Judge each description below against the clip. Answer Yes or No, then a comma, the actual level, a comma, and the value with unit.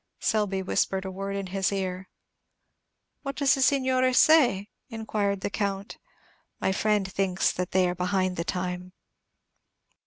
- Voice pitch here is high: Yes, high, 195 Hz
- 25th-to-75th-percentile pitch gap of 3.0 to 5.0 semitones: No, narrow, 2.6 semitones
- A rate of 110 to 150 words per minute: Yes, average, 145 wpm